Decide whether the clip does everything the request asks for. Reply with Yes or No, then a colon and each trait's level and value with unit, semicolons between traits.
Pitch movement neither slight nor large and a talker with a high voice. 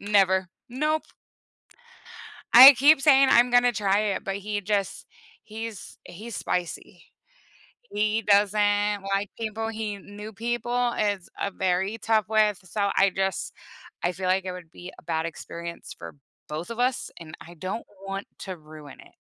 Yes: average, 3.2 semitones; high, 205 Hz